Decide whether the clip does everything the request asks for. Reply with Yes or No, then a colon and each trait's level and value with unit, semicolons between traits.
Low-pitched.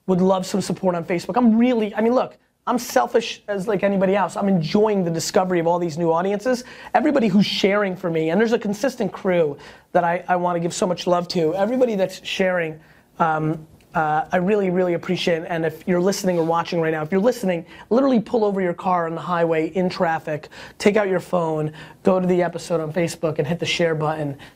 No: medium, 180 Hz